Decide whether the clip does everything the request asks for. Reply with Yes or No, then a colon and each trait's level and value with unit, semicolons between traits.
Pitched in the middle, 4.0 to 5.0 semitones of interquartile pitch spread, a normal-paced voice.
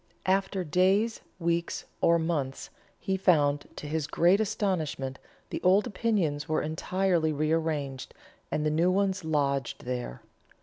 No: medium, 165 Hz; average, 4.4 semitones; slow, 130 wpm